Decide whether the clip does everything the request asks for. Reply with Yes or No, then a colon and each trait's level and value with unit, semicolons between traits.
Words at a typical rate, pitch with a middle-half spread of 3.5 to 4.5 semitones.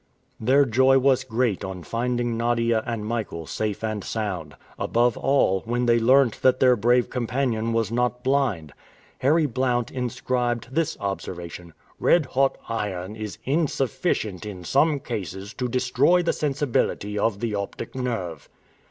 Yes: average, 145 wpm; average, 3.8 semitones